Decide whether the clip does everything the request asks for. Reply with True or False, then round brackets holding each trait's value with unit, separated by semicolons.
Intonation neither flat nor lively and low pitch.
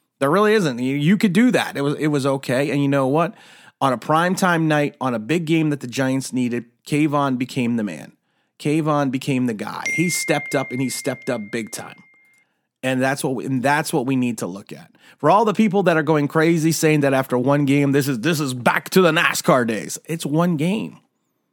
False (3.6 semitones; 145 Hz)